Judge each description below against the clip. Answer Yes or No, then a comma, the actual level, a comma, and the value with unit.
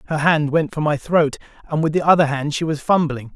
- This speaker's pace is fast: Yes, fast, 250 wpm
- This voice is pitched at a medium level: Yes, medium, 150 Hz